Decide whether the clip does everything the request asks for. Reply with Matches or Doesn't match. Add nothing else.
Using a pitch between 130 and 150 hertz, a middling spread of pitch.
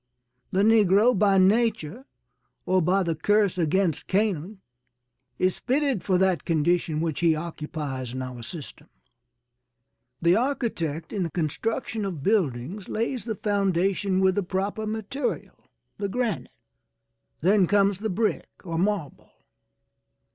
Doesn't match